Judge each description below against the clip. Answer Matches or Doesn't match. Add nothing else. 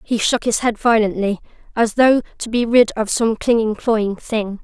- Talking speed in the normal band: Matches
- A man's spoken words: Doesn't match